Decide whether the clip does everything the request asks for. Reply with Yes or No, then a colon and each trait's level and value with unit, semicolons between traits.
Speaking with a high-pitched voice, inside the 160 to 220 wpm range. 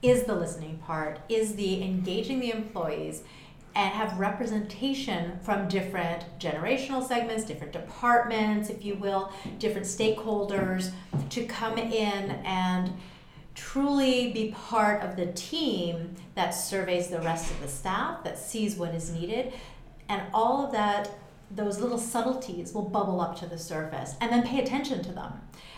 No: high, 200 Hz; average, 150 wpm